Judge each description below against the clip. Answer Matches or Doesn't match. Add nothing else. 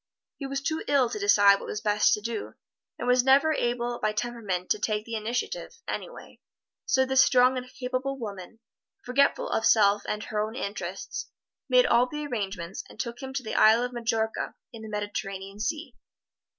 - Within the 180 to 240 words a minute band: Matches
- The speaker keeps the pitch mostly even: Doesn't match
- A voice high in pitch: Matches